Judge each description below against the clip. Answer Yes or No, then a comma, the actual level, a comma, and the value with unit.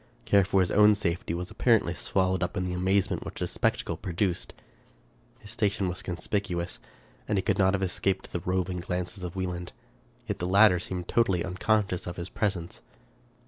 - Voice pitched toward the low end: Yes, very low, 90 Hz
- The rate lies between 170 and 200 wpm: Yes, average, 185 wpm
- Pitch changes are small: Yes, narrow, 1.9 semitones